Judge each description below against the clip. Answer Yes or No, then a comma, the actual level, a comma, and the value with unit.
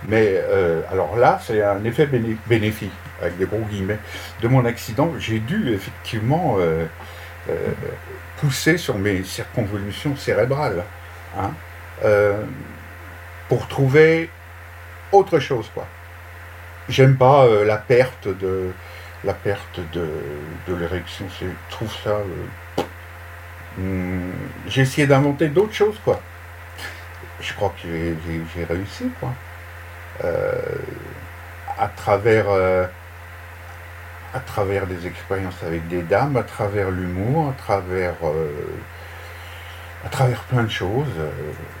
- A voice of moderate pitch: No, very low, 90 Hz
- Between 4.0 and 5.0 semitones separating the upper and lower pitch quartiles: Yes, average, 4.3 semitones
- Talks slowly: Yes, slow, 120 wpm